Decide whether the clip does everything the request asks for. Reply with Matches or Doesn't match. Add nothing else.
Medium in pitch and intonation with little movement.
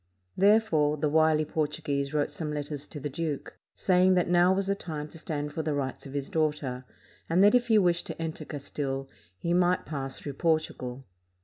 Doesn't match